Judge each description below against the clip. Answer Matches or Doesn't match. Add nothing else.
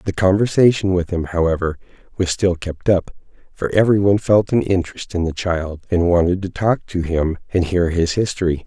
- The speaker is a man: Matches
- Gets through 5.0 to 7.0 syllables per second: Matches